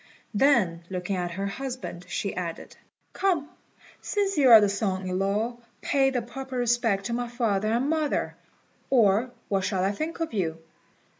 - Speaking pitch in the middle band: No, high, 225 Hz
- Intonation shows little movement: No, average, 5.3 semitones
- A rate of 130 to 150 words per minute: No, average, 165 wpm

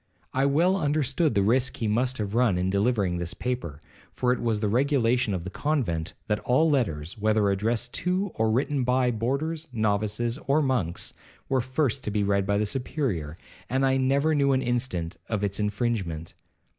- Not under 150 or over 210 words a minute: Yes, average, 180 wpm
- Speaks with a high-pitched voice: No, low, 120 Hz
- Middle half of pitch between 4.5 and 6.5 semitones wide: Yes, average, 4.8 semitones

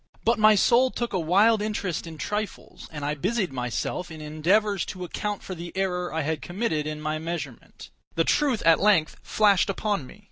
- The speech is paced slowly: No, average, 190 wpm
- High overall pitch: No, medium, 180 Hz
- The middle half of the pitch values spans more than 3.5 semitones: Yes, average, 5.0 semitones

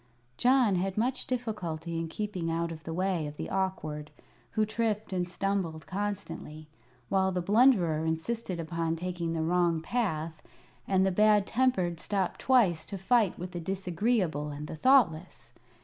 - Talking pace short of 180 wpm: Yes, average, 155 wpm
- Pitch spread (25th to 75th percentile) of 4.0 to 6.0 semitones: Yes, average, 4.3 semitones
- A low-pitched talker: No, medium, 180 Hz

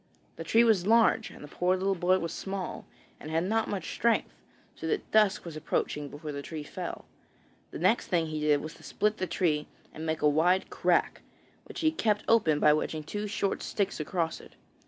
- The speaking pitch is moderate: Yes, medium, 175 Hz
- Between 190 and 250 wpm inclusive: Yes, fast, 205 wpm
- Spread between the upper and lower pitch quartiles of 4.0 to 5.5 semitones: Yes, average, 5.0 semitones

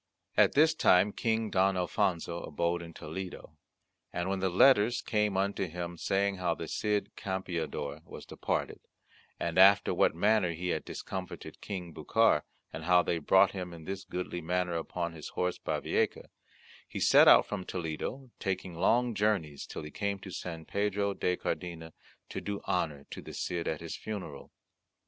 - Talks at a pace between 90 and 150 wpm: No, average, 170 wpm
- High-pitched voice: No, very low, 90 Hz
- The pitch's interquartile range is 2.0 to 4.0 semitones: Yes, average, 2.9 semitones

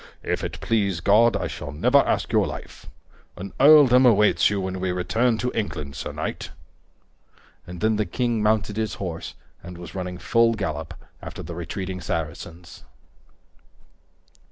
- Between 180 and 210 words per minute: No, average, 155 wpm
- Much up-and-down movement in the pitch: No, average, 4.5 semitones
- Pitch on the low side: Yes, low, 100 Hz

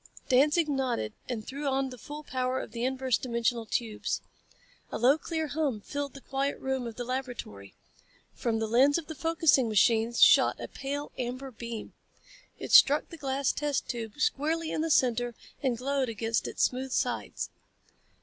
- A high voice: Yes, very high, 260 Hz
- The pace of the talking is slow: No, average, 170 wpm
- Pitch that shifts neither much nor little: Yes, average, 3.3 semitones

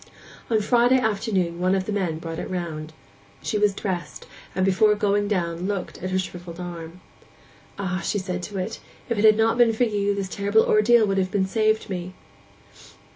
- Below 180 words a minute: No, average, 190 wpm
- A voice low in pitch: No, high, 195 Hz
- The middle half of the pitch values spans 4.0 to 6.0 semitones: No, average, 2.9 semitones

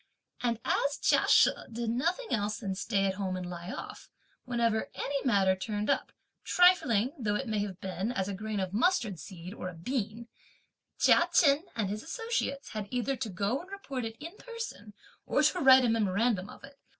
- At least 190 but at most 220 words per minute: Yes, average, 195 wpm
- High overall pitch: Yes, high, 225 Hz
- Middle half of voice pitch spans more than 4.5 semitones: Yes, average, 5.2 semitones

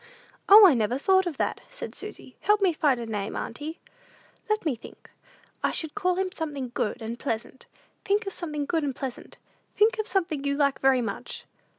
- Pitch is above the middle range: Yes, very high, 300 Hz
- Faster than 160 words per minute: Yes, average, 195 wpm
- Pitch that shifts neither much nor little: No, wide, 6.7 semitones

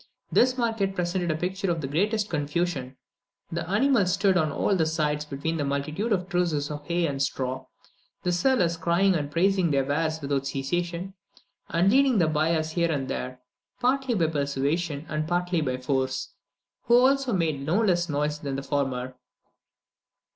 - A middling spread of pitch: Yes, average, 4.6 semitones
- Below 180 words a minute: Yes, average, 165 wpm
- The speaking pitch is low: No, medium, 165 Hz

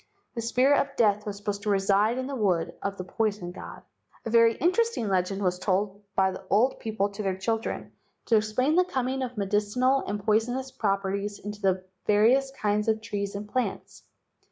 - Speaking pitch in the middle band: No, high, 210 Hz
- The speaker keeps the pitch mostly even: No, average, 3.5 semitones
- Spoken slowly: No, average, 185 wpm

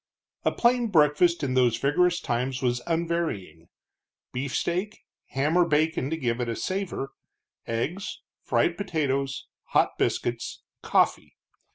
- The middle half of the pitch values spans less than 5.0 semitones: No, wide, 5.5 semitones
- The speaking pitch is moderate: Yes, medium, 145 Hz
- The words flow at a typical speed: No, slow, 125 wpm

